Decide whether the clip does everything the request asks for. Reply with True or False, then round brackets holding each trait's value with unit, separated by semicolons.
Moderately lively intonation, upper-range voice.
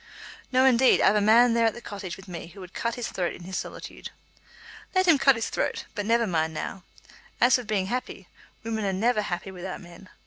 True (4.1 semitones; 210 Hz)